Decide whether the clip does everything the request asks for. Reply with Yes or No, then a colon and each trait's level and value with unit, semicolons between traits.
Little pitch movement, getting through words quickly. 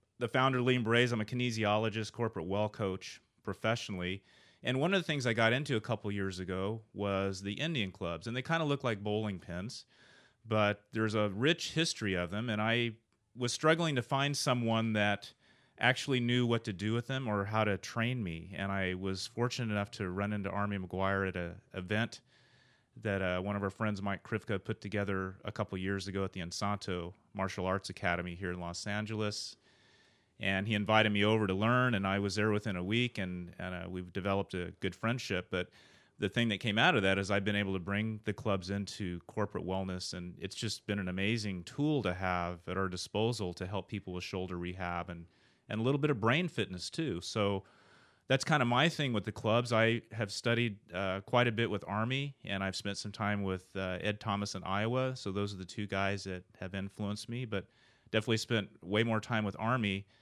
No: average, 3.2 semitones; fast, 215 wpm